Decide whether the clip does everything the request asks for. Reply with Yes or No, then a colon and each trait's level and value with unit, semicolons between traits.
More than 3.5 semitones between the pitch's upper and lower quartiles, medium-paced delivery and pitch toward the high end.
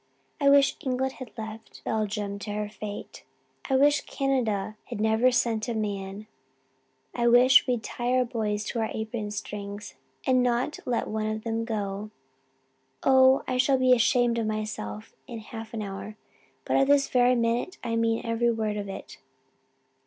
No: average, 3.0 semitones; average, 165 wpm; high, 225 Hz